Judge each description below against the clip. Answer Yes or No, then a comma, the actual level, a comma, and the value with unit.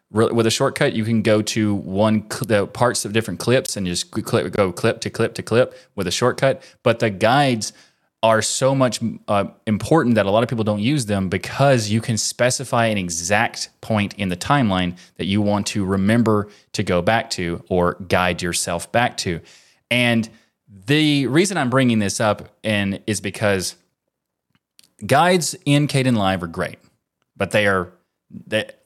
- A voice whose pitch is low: Yes, low, 110 Hz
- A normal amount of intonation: Yes, average, 3.4 semitones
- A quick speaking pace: No, average, 180 wpm